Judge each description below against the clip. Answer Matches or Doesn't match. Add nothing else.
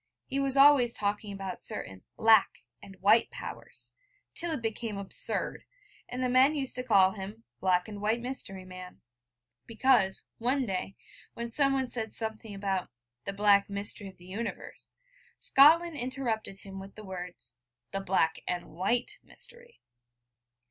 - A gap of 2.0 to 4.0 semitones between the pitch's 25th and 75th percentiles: Doesn't match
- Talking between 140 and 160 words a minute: Matches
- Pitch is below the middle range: Doesn't match